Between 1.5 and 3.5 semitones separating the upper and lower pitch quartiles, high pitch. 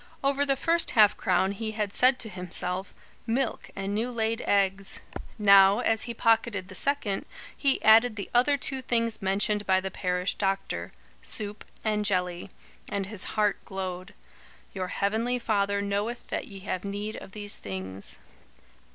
Yes: average, 2.9 semitones; high, 205 Hz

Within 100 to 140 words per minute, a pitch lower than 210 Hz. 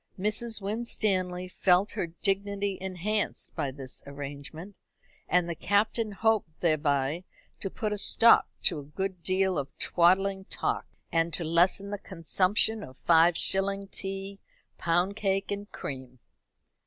Yes: slow, 135 wpm; high, 190 Hz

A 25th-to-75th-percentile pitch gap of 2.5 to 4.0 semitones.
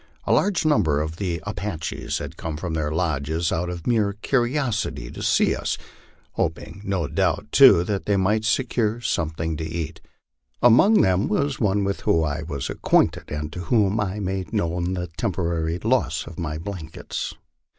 No: average, 4.6 semitones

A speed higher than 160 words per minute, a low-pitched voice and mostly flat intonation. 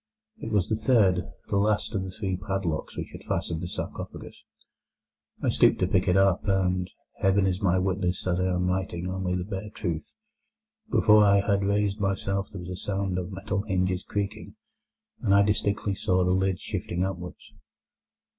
Yes: average, 175 wpm; very low, 95 Hz; narrow, 1.8 semitones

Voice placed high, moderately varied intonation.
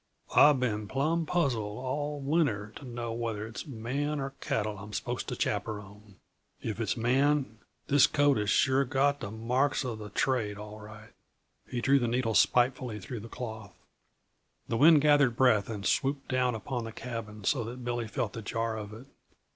No: low, 120 Hz; average, 4.0 semitones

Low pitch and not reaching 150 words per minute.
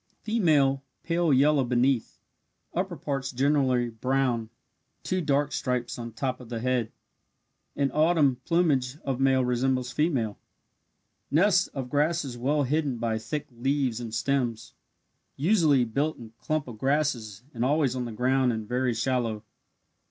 Yes: low, 130 Hz; average, 140 wpm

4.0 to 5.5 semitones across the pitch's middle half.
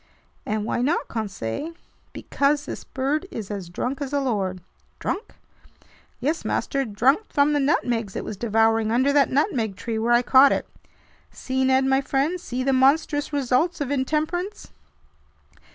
Yes: average, 4.3 semitones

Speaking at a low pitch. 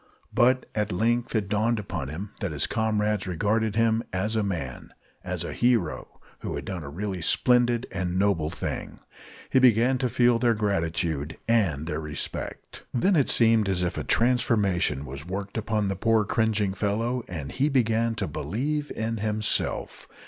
Yes: low, 105 Hz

